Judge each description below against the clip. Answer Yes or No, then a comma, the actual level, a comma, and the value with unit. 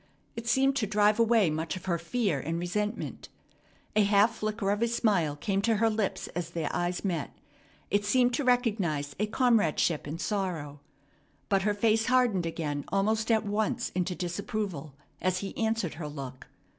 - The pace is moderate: Yes, average, 170 wpm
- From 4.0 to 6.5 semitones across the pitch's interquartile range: Yes, average, 4.7 semitones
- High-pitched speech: Yes, high, 200 Hz